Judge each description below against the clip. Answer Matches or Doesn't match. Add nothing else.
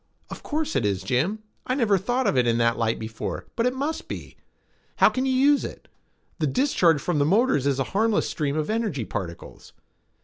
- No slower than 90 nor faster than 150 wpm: Doesn't match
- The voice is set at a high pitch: Doesn't match